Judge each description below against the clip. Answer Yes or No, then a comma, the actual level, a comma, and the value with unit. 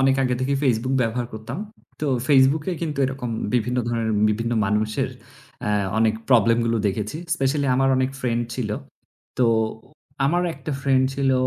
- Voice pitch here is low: Yes, low, 125 Hz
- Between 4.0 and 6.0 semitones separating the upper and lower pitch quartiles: No, average, 2.8 semitones